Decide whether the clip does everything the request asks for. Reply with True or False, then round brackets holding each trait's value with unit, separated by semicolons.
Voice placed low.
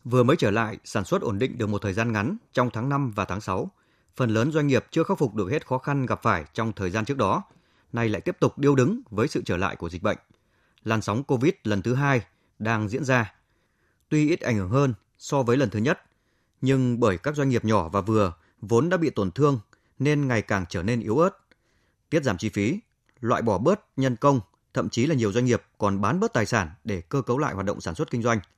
True (120 Hz)